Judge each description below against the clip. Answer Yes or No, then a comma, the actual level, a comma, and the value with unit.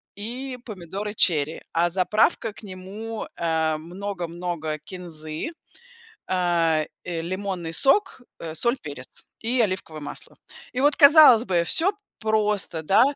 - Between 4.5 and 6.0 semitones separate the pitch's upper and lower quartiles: Yes, average, 4.8 semitones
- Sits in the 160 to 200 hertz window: Yes, medium, 185 Hz